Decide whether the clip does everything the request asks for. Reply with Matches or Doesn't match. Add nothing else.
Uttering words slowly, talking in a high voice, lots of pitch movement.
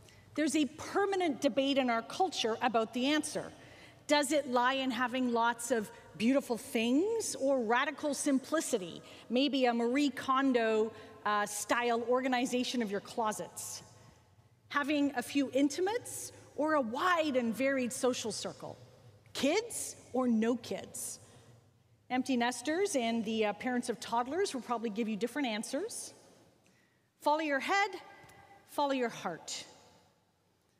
Doesn't match